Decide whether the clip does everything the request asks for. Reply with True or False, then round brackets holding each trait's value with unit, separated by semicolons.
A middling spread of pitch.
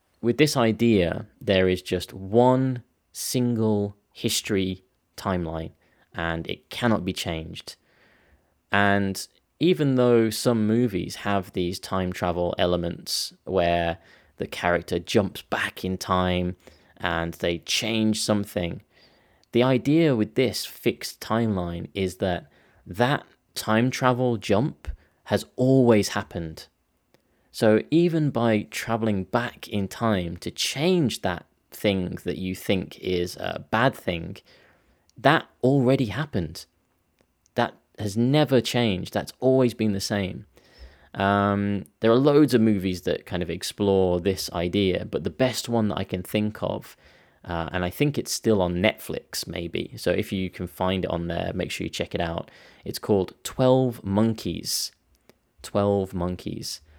True (4.7 semitones)